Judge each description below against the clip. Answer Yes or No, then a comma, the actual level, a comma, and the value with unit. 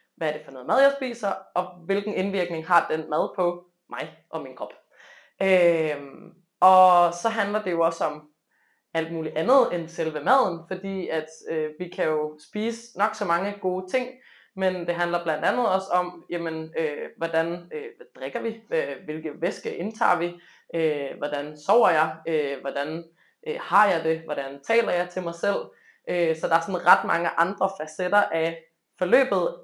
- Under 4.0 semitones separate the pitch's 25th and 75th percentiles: Yes, average, 3.3 semitones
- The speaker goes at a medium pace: Yes, average, 180 wpm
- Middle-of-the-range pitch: Yes, medium, 175 Hz